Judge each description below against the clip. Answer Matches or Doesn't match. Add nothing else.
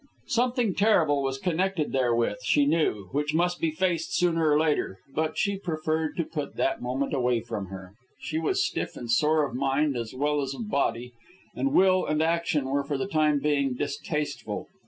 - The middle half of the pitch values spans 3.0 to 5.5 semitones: Matches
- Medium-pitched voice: Matches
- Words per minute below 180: Doesn't match